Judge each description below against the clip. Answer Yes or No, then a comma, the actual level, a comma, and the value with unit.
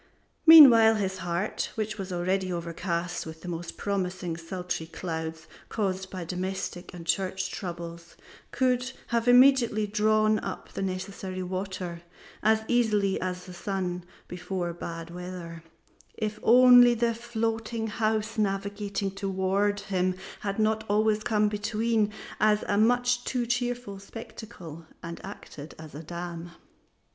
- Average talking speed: No, slow, 130 wpm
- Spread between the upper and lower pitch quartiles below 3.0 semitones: No, average, 3.6 semitones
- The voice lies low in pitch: No, high, 195 Hz